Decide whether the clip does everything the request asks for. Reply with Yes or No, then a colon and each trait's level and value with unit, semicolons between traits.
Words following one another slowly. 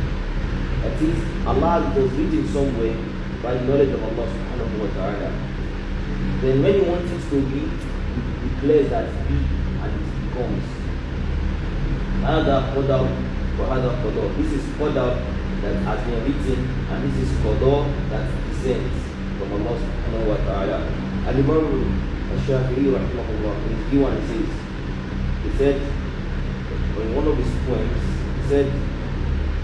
Yes: slow, 115 wpm